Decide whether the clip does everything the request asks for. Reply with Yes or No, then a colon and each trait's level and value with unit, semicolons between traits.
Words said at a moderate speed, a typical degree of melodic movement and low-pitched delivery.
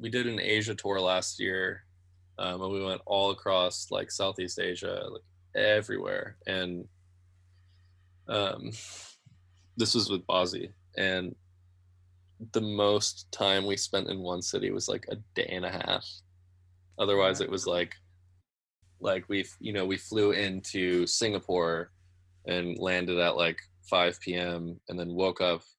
No: average, 145 wpm; narrow, 1.4 semitones; very low, 90 Hz